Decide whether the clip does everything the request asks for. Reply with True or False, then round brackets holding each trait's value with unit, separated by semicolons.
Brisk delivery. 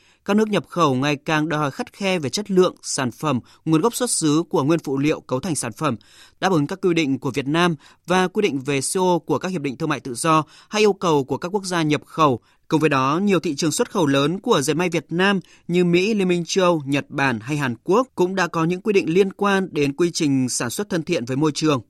True (270 wpm)